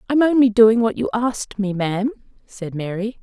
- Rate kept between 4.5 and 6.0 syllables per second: Yes, 5.7 syllables/s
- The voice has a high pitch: Yes, high, 220 Hz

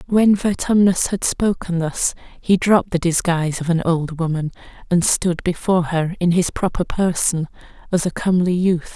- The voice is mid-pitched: Yes, medium, 175 Hz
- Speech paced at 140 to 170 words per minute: Yes, average, 165 wpm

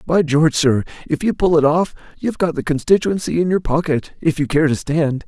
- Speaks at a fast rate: Yes, fast, 230 wpm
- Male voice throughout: Yes, male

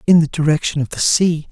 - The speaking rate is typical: No, fast, 235 wpm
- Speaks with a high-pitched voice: No, medium, 160 Hz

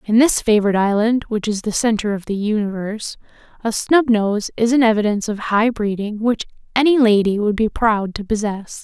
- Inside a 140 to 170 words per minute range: No, average, 185 wpm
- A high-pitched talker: Yes, high, 215 Hz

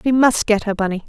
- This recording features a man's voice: No, female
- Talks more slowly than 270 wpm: No, fast, 280 wpm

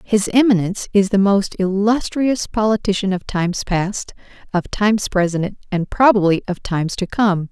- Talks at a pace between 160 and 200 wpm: No, average, 150 wpm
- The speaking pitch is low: No, high, 200 Hz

